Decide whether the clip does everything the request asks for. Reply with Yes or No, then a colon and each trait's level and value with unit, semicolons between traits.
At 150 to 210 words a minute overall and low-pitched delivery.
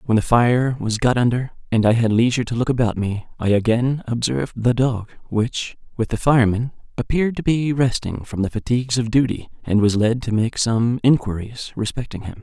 Yes: average, 200 wpm; low, 120 Hz